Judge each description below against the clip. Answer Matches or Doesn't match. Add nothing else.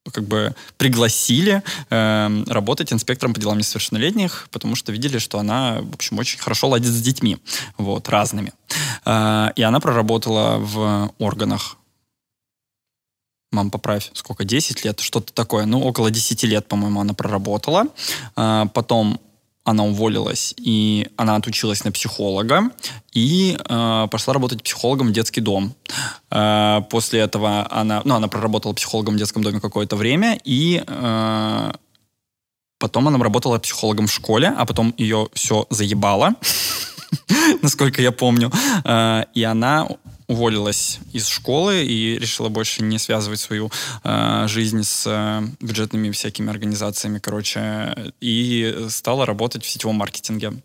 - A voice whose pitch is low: Matches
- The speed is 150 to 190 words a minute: Doesn't match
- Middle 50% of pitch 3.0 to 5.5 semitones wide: Doesn't match